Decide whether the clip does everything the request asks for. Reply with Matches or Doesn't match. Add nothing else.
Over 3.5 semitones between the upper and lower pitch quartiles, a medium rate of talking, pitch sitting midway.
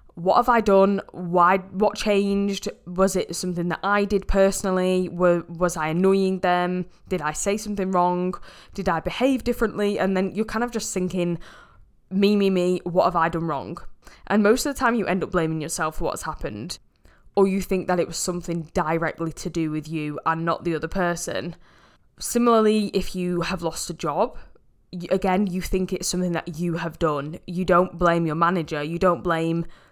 Doesn't match